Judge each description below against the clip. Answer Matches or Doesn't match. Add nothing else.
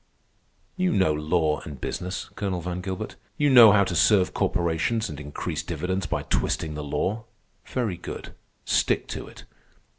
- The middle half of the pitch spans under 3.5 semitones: Doesn't match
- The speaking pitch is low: Matches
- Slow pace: Doesn't match